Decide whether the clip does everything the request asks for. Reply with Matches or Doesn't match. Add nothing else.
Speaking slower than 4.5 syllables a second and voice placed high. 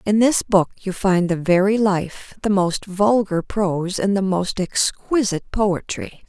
Matches